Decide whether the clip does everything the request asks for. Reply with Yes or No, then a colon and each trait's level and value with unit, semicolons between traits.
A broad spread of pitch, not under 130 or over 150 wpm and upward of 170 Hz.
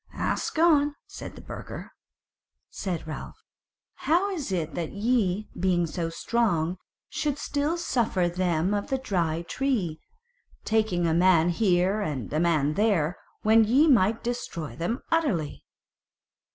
Yes: wide, 6.4 semitones; slow, 135 wpm; high, 190 Hz